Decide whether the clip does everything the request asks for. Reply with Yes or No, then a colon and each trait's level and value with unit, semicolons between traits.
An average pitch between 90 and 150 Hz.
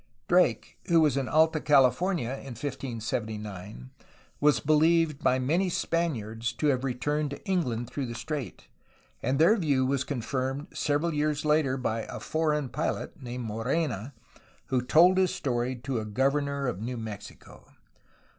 Yes: low, 135 Hz